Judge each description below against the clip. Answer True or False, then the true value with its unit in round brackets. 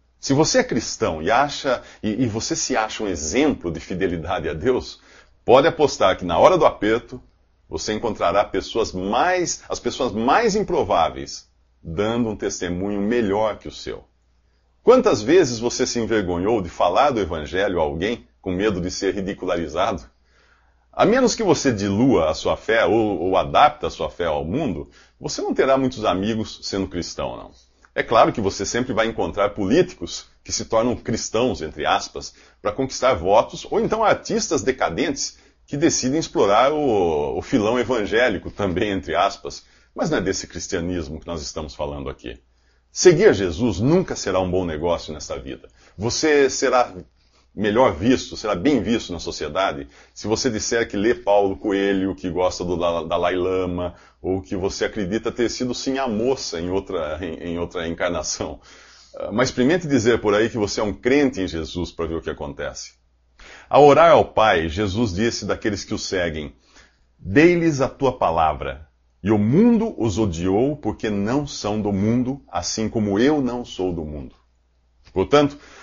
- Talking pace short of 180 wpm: True (170 wpm)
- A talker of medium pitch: False (100 Hz)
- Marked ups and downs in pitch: True (5.9 semitones)